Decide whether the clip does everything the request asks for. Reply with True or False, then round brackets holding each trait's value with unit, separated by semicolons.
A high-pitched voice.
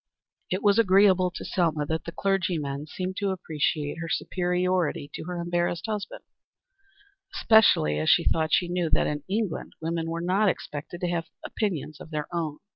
False (175 Hz)